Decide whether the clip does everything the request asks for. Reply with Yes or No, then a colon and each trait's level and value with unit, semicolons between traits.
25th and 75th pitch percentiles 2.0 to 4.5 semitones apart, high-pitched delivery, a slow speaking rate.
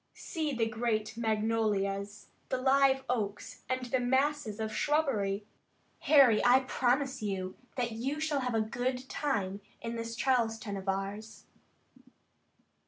Yes: average, 3.8 semitones; high, 230 Hz; slow, 130 wpm